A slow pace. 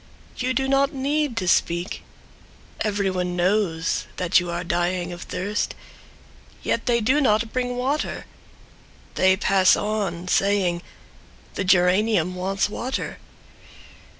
Yes: slow, 120 wpm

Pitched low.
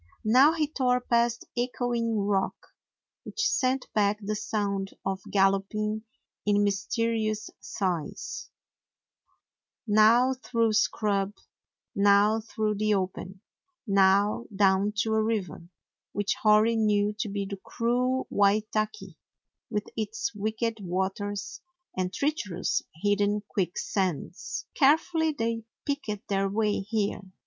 No: high, 210 Hz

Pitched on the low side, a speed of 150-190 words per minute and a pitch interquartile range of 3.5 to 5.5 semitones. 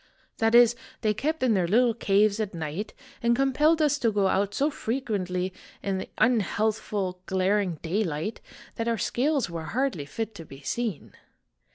No: high, 215 Hz; average, 165 wpm; average, 4.4 semitones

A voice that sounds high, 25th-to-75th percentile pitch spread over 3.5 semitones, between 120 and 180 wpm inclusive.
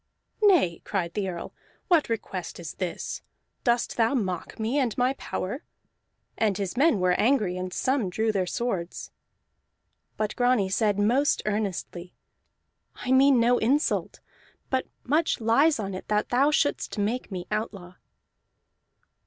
Yes: high, 220 Hz; average, 5.3 semitones; average, 140 wpm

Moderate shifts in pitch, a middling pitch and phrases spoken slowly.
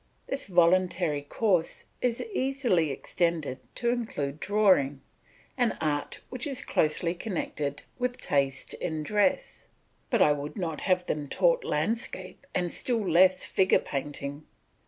No: wide, 7.2 semitones; medium, 180 Hz; slow, 130 wpm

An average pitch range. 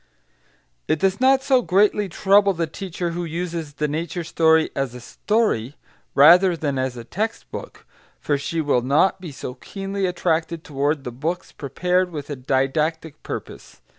Yes: average, 4.6 semitones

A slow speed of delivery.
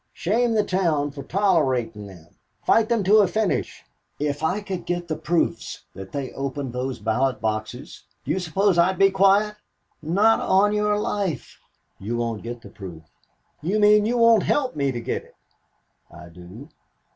No: average, 170 wpm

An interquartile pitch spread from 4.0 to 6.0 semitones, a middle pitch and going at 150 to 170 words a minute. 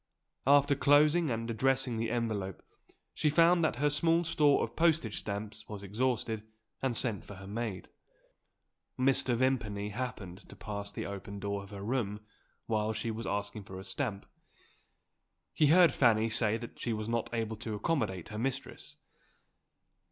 No: average, 4.4 semitones; low, 115 Hz; average, 160 wpm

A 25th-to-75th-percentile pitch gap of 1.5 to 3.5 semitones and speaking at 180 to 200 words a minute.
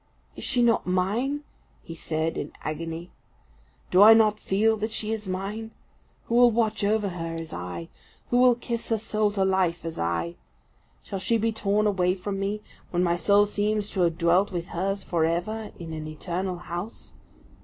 No: average, 4.2 semitones; average, 185 wpm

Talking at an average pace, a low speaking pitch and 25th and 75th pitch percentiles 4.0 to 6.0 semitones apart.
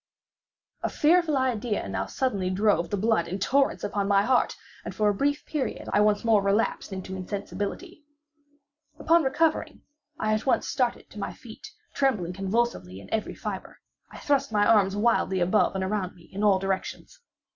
No: average, 170 wpm; high, 210 Hz; average, 5.1 semitones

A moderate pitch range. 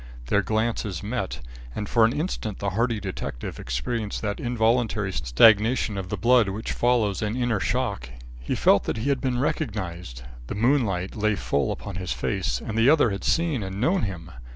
Yes: average, 4.2 semitones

